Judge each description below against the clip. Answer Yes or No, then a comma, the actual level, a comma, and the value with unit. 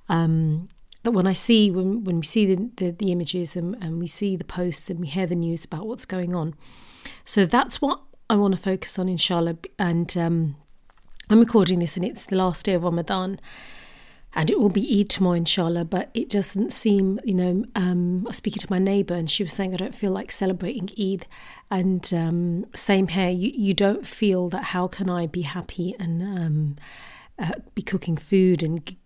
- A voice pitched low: No, medium, 185 Hz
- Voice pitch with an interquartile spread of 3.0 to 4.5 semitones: No, narrow, 2.6 semitones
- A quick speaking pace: Yes, fast, 210 wpm